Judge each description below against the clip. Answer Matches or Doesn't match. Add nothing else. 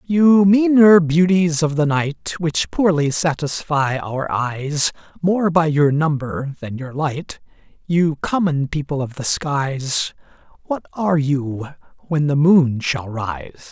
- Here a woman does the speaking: Doesn't match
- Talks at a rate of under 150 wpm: Matches